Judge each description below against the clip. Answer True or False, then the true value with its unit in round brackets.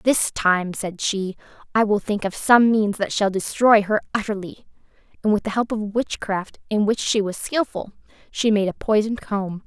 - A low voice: False (210 Hz)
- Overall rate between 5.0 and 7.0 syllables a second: False (4.7 syllables/s)